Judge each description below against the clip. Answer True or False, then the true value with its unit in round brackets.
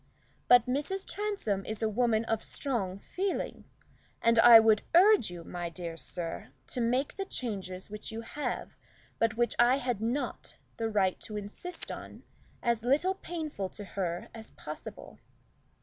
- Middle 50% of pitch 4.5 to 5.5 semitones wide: True (4.9 semitones)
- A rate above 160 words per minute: False (155 wpm)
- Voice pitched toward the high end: True (225 Hz)